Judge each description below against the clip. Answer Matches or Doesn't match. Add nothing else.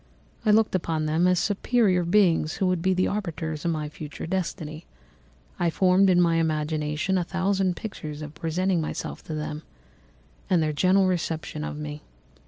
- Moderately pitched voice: Matches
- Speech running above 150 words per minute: Matches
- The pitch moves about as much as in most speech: Matches